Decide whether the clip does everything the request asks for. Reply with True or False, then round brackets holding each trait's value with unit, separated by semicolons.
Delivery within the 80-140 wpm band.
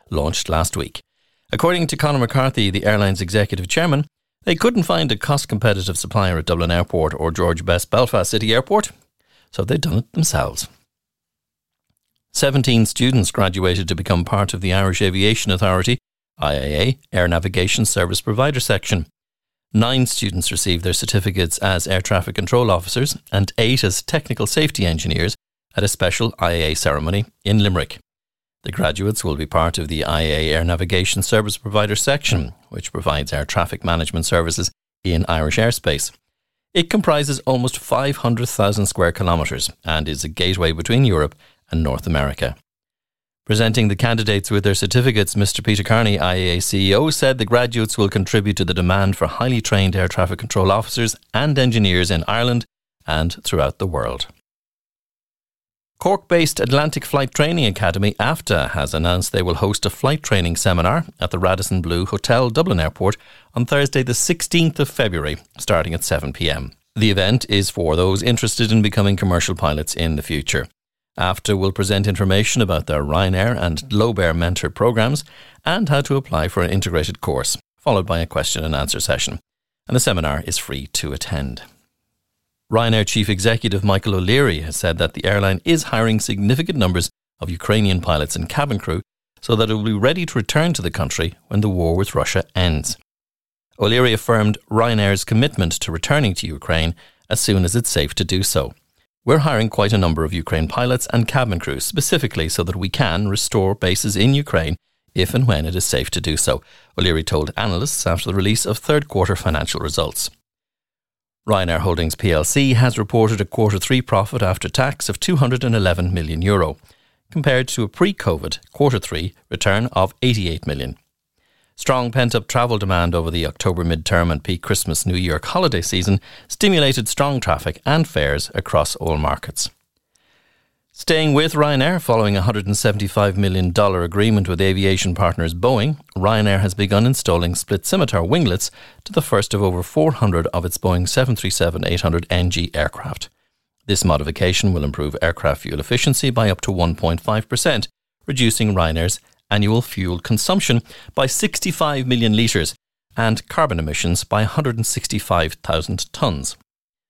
False (160 wpm)